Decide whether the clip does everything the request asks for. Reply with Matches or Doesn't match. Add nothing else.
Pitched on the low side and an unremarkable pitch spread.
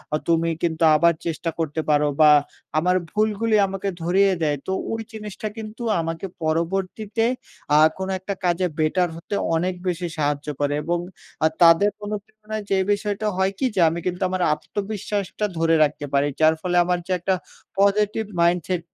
Doesn't match